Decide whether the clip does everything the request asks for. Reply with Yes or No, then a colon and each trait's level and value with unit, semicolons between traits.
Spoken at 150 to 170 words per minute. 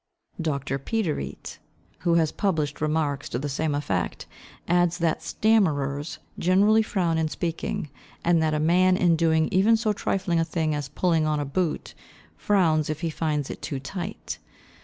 Yes: average, 160 wpm